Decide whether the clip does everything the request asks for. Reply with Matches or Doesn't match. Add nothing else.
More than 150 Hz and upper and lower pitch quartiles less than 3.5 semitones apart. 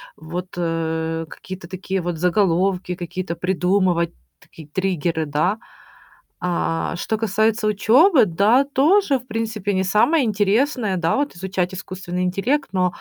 Doesn't match